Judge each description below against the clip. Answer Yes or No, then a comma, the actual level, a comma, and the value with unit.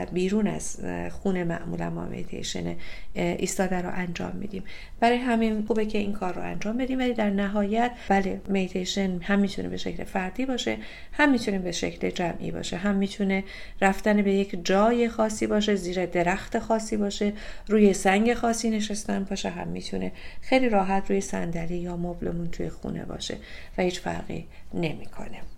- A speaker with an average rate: No, fast, 160 wpm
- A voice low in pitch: No, high, 195 Hz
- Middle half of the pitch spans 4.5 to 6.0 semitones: No, average, 3.3 semitones